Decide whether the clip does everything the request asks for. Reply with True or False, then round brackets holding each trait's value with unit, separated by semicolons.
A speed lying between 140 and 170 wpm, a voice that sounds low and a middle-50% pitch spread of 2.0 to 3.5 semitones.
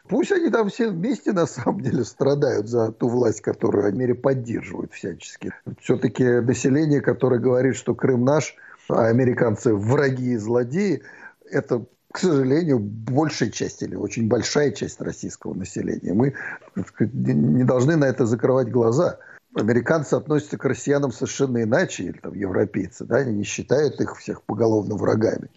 True (150 wpm; 130 Hz; 3.0 semitones)